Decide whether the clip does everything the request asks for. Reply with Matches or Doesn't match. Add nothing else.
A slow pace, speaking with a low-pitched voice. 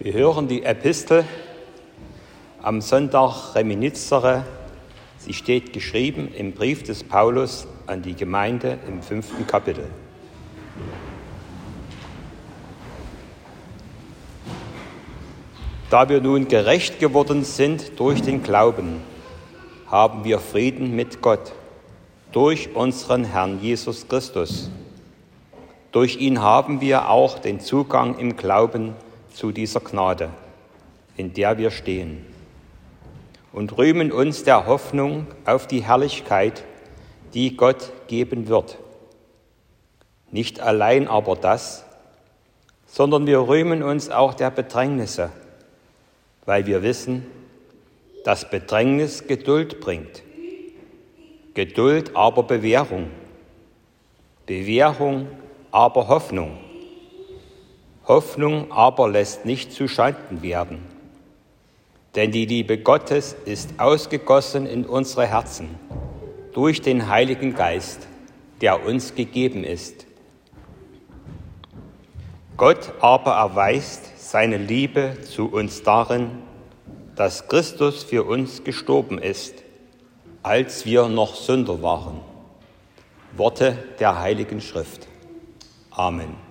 Matches